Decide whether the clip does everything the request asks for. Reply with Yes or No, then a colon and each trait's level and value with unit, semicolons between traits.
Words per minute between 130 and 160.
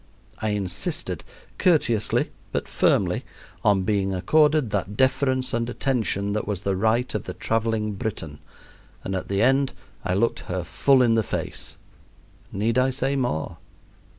Yes: average, 150 wpm